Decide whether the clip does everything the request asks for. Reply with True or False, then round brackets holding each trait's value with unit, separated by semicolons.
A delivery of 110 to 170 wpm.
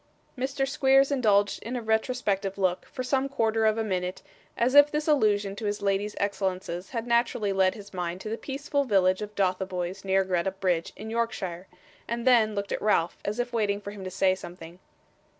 False (195 wpm)